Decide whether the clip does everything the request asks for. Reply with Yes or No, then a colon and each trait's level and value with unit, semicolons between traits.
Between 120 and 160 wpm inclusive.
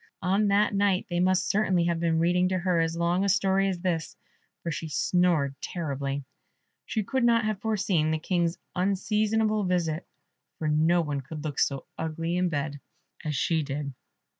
No: average, 175 wpm